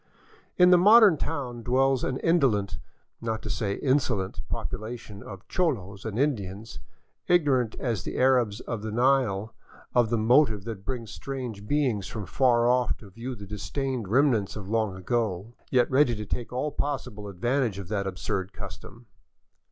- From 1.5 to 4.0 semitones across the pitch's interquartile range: No, average, 4.4 semitones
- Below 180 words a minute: Yes, average, 160 wpm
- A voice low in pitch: Yes, low, 115 Hz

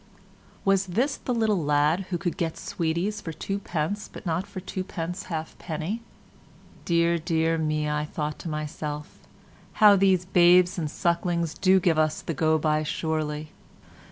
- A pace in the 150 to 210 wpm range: Yes, average, 155 wpm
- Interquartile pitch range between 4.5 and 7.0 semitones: No, average, 3.2 semitones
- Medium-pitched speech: Yes, medium, 170 Hz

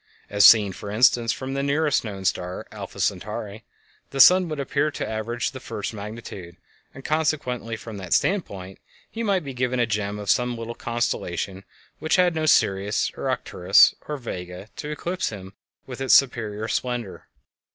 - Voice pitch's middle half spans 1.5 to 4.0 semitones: No, average, 5.3 semitones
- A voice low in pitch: Yes, low, 120 Hz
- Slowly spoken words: No, average, 165 wpm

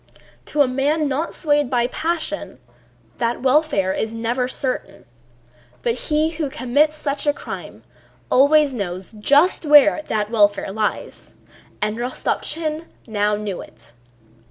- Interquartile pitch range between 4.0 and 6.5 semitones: Yes, wide, 5.6 semitones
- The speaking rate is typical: No, slow, 130 wpm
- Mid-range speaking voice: No, very high, 260 Hz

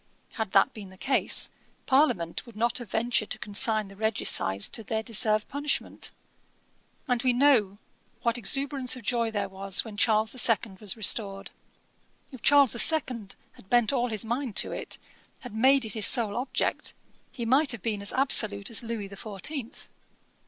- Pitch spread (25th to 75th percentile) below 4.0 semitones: Yes, average, 3.5 semitones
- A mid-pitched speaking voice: No, high, 225 Hz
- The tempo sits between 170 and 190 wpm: Yes, average, 175 wpm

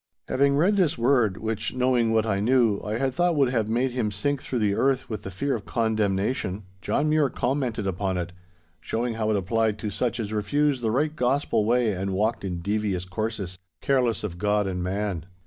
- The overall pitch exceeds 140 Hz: No, low, 110 Hz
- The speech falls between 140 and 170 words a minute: No, fast, 205 wpm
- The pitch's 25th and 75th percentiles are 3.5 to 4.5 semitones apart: Yes, average, 4.1 semitones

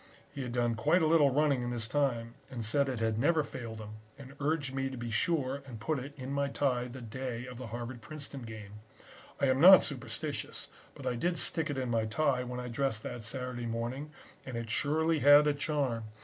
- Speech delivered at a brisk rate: Yes, fast, 220 wpm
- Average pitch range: Yes, average, 3.5 semitones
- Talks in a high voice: No, low, 130 Hz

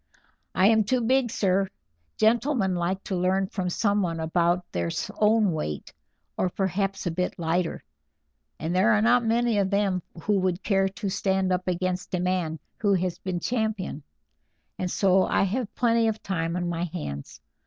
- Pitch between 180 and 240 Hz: Yes, high, 190 Hz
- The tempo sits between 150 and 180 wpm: Yes, average, 170 wpm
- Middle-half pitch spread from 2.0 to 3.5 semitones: Yes, average, 2.9 semitones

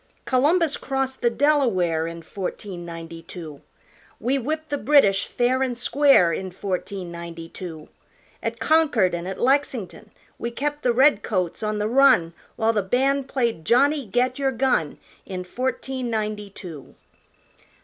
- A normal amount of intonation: No, wide, 6.8 semitones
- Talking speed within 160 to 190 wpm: No, average, 145 wpm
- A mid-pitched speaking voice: No, high, 225 Hz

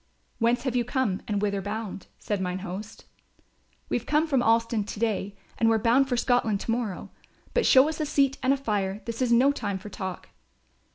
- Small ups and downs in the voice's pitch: No, average, 4.0 semitones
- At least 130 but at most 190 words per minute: No, fast, 205 wpm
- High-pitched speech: Yes, high, 230 Hz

